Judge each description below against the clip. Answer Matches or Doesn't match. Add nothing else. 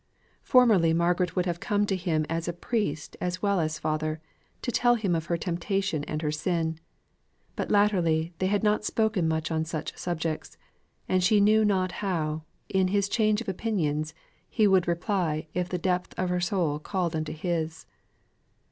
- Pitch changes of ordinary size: Matches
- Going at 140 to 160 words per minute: Doesn't match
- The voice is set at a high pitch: Doesn't match